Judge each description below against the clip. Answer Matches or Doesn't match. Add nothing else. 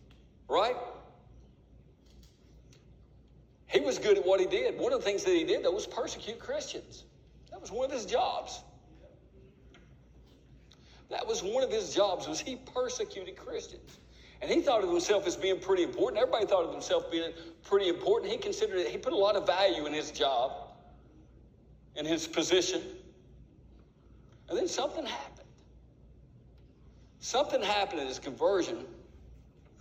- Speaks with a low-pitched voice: Doesn't match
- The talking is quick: Doesn't match